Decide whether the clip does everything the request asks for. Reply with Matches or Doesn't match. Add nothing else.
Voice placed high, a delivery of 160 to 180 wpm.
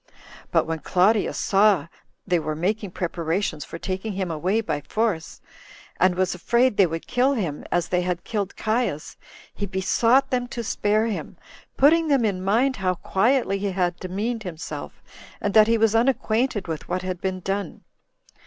Matches